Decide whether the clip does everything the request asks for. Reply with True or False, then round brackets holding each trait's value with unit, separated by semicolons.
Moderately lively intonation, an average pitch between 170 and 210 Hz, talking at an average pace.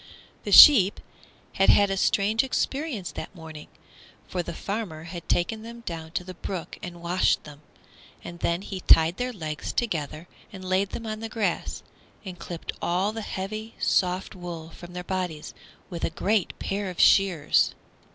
True (3.4 semitones; 185 Hz; 170 wpm)